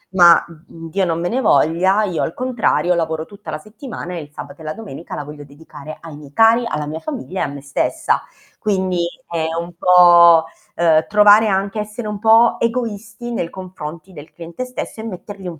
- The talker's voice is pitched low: No, medium, 180 Hz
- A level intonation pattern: No, average, 4.7 semitones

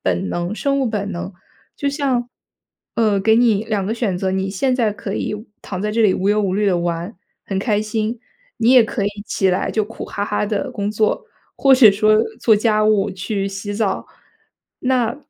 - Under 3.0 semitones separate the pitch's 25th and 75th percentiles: Yes, narrow, 2.5 semitones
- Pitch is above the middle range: Yes, high, 210 Hz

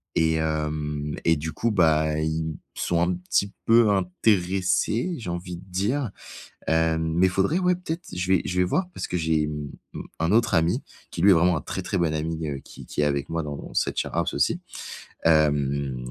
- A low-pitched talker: Yes, very low, 85 Hz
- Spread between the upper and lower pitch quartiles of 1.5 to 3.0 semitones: No, average, 3.5 semitones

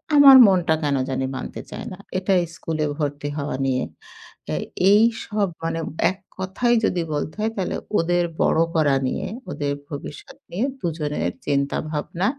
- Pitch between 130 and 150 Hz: No, medium, 160 Hz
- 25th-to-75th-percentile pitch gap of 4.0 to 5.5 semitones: Yes, average, 4.8 semitones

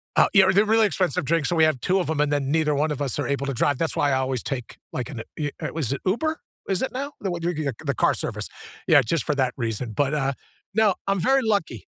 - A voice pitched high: No, medium, 150 Hz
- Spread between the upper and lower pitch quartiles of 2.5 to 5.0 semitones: No, wide, 5.6 semitones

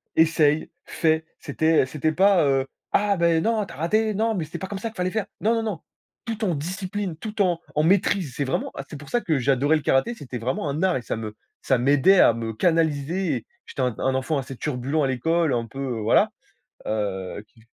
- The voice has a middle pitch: Yes, medium, 155 Hz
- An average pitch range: No, wide, 6.1 semitones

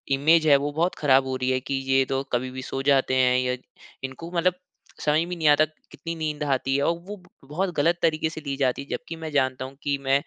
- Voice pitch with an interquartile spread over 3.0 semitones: Yes, average, 3.4 semitones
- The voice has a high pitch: No, medium, 145 Hz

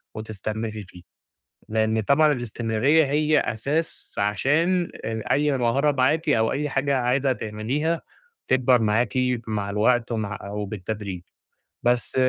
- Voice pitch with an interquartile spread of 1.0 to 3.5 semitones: No, average, 4.6 semitones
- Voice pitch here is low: Yes, low, 120 Hz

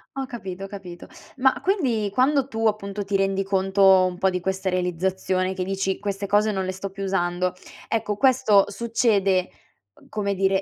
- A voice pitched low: No, high, 195 Hz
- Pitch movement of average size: No, narrow, 2.1 semitones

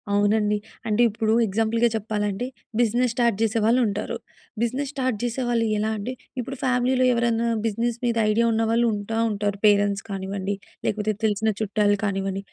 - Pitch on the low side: No, high, 220 Hz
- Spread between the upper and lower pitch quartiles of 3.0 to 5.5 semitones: No, narrow, 2.6 semitones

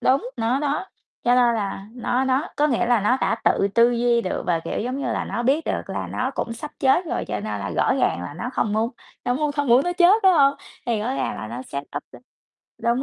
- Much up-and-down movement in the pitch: No, average, 4.2 semitones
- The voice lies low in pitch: No, high, 245 Hz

